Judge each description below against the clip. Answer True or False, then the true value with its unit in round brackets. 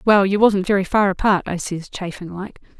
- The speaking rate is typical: False (215 wpm)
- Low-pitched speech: False (190 Hz)